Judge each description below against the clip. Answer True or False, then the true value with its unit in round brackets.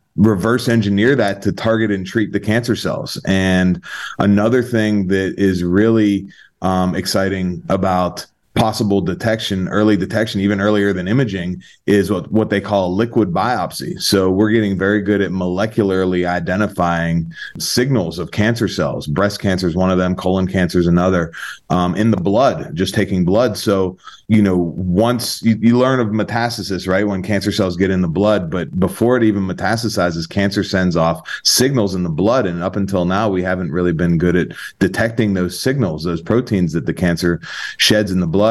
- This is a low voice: True (100 Hz)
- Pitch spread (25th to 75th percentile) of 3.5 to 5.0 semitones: False (2.9 semitones)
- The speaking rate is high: False (180 wpm)